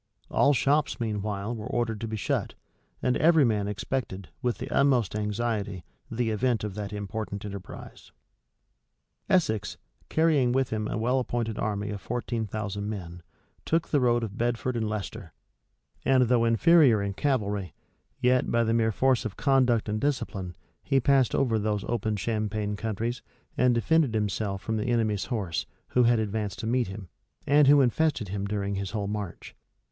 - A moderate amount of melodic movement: Yes, average, 3.4 semitones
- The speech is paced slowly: No, average, 165 wpm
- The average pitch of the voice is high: No, low, 110 Hz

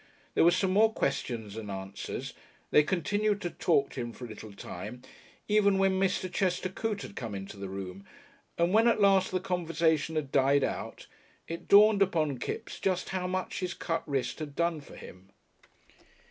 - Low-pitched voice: No, medium, 170 Hz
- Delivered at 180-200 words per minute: Yes, average, 185 wpm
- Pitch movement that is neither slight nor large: No, wide, 7.2 semitones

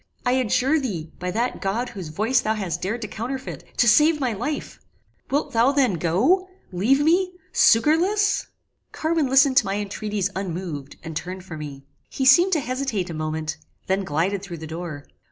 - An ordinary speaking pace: Yes, average, 175 wpm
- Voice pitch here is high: Yes, high, 215 Hz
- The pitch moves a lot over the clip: Yes, wide, 7.3 semitones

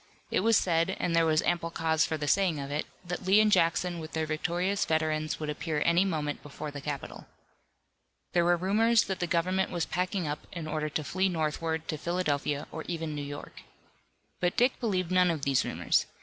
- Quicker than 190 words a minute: Yes, fast, 205 wpm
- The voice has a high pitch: No, medium, 165 Hz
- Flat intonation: No, average, 3.0 semitones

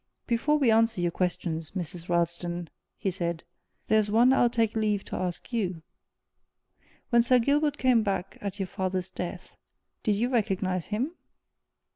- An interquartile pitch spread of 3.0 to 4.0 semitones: No, average, 4.7 semitones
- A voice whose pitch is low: No, high, 200 Hz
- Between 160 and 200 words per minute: No, average, 150 wpm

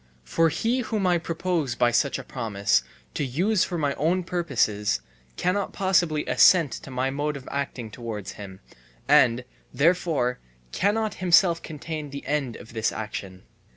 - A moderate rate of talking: Yes, average, 155 wpm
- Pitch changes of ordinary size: No, wide, 6.4 semitones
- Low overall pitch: No, medium, 145 Hz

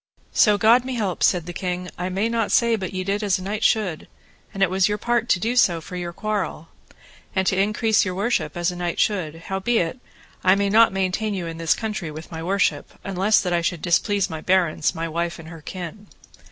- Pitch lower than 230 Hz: Yes, high, 190 Hz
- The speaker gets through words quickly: Yes, fast, 225 wpm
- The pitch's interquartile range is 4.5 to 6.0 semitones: No, average, 3.5 semitones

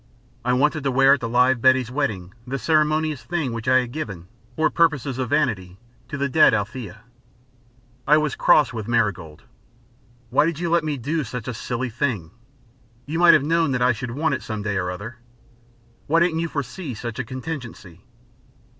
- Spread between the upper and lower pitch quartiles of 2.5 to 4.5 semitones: No, average, 5.0 semitones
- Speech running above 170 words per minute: Yes, average, 190 wpm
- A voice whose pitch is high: No, low, 130 Hz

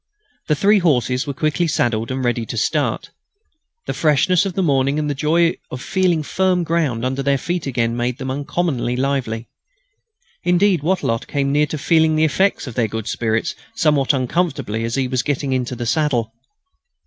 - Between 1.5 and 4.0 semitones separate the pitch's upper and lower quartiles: No, average, 4.8 semitones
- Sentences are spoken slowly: No, average, 175 wpm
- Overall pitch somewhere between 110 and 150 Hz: Yes, medium, 140 Hz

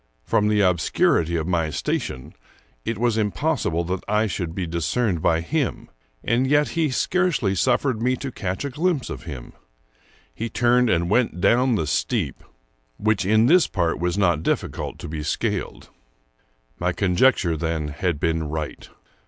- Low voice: Yes, very low, 95 Hz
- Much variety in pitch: Yes, wide, 6.6 semitones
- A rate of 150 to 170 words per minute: Yes, average, 160 wpm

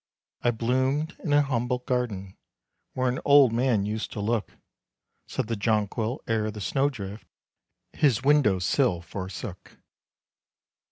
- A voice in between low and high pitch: No, low, 115 Hz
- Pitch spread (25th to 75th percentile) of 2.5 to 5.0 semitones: Yes, average, 3.9 semitones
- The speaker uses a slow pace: Yes, slow, 130 wpm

